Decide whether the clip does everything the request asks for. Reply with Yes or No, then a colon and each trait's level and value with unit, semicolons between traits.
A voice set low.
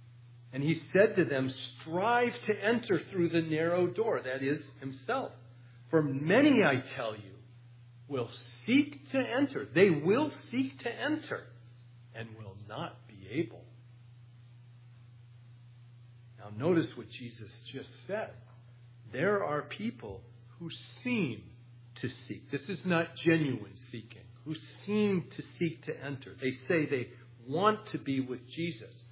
Yes: low, 130 Hz